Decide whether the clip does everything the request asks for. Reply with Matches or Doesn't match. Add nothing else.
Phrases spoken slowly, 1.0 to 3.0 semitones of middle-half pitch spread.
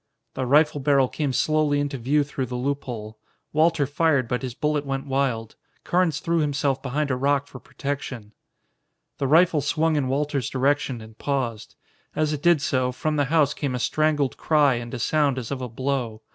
Doesn't match